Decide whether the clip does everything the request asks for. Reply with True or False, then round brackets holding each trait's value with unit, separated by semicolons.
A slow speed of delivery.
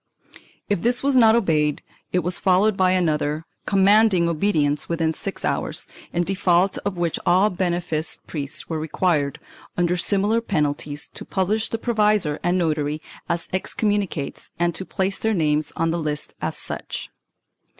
False (160 wpm)